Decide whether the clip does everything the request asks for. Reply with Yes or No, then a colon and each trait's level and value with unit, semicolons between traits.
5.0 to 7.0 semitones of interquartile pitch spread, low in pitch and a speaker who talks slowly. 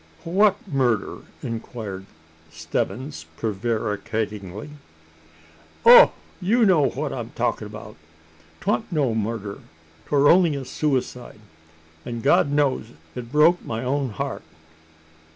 Yes: average, 5.3 semitones; low, 125 Hz; slow, 105 wpm